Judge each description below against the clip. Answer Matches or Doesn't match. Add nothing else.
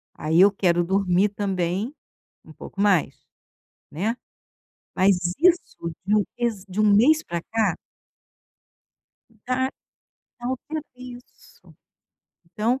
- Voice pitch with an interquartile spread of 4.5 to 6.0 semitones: Matches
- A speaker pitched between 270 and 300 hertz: Doesn't match